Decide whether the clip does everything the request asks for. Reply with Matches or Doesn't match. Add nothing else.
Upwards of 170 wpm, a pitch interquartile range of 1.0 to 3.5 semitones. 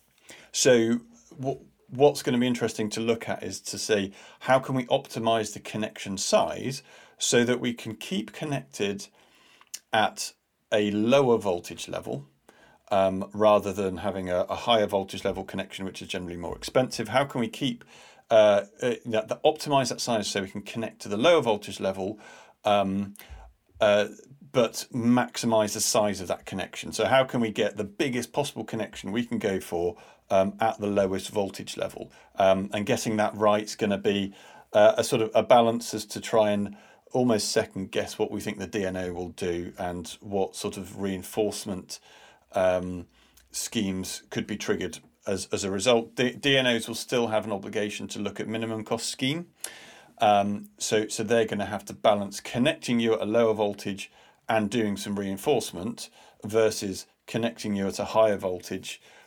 Matches